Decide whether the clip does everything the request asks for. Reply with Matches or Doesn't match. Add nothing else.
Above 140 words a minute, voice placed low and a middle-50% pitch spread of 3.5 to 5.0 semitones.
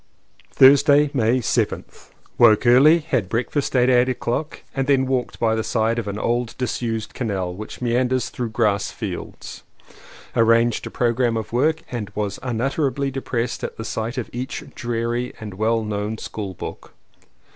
Doesn't match